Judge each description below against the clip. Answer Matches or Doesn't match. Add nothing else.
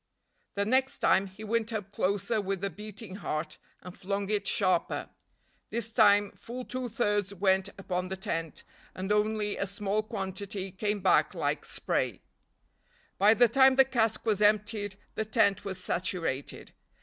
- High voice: Matches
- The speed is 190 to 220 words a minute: Doesn't match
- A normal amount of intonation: Doesn't match